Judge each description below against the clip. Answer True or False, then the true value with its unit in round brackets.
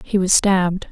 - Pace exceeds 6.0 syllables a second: False (4.9 syllables/s)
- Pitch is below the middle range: False (185 Hz)